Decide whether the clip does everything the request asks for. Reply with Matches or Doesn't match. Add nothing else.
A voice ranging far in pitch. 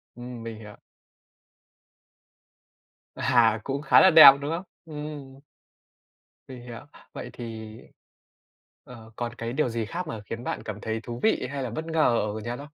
Doesn't match